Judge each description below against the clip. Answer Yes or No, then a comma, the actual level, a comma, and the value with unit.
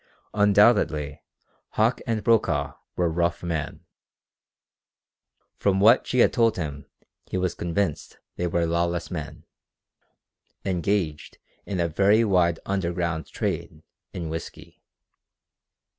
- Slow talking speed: Yes, slow, 110 wpm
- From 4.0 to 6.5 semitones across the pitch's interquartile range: No, average, 3.3 semitones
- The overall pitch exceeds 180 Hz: No, very low, 85 Hz